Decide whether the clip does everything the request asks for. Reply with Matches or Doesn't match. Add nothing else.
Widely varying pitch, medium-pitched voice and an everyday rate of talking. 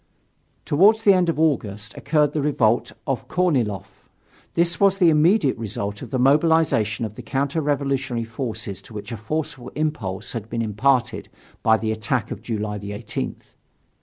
Doesn't match